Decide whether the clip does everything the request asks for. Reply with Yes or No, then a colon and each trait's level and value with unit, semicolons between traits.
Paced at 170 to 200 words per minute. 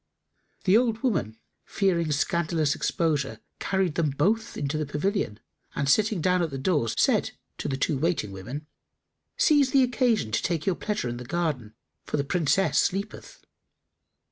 No: average, 160 wpm